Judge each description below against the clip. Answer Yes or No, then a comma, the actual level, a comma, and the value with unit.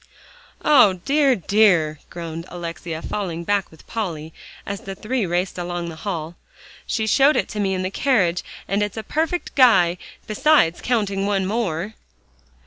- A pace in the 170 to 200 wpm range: No, average, 155 wpm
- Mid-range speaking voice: No, high, 195 Hz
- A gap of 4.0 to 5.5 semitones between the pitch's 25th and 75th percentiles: Yes, average, 4.3 semitones